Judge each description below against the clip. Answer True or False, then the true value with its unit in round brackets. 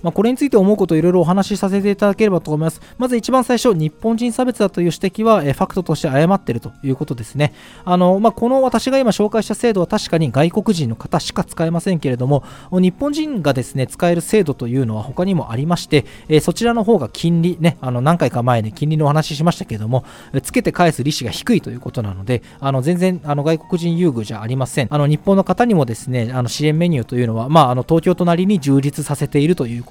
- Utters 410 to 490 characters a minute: True (430 characters per minute)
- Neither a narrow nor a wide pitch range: False (6.4 semitones)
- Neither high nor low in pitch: True (165 Hz)